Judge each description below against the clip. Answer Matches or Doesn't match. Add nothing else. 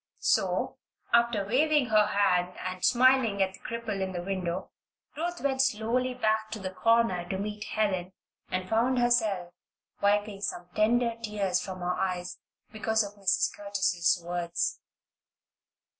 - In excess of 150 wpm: Doesn't match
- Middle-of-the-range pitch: Doesn't match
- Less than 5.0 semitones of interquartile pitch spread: Matches